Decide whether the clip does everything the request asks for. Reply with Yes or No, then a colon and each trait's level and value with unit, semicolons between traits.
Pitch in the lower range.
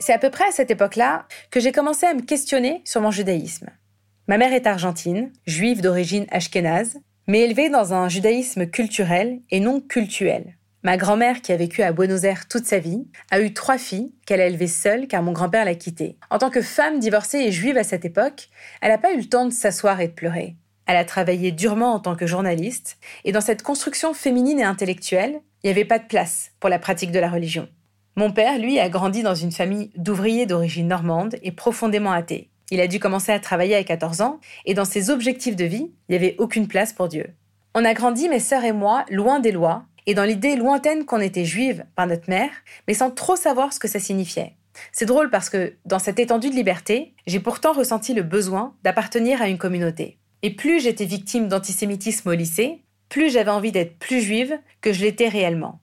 No: high, 210 Hz